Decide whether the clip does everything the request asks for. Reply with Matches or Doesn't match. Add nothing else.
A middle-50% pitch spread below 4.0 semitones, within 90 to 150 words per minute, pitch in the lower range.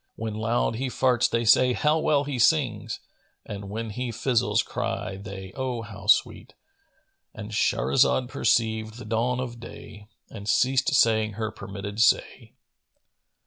Matches